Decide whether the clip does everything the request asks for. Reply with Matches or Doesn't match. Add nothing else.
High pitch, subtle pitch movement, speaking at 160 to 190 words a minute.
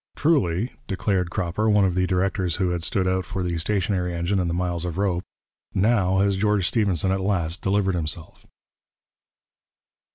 Doesn't match